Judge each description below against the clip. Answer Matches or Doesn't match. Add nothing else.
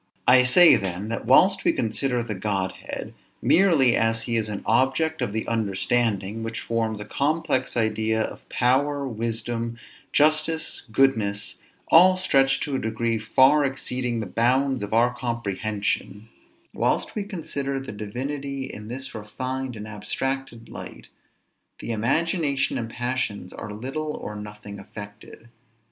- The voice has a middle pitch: Doesn't match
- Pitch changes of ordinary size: Matches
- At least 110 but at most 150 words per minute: Matches